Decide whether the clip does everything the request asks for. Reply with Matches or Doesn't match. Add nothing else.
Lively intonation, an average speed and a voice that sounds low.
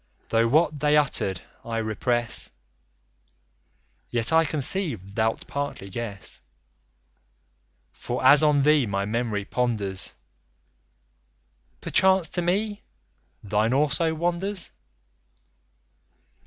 Doesn't match